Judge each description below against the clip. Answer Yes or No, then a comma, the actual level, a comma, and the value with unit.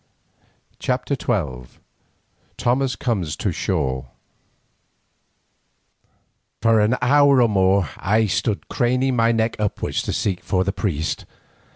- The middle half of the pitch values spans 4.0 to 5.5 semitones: Yes, average, 4.8 semitones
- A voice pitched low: Yes, low, 110 Hz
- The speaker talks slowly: Yes, slow, 115 wpm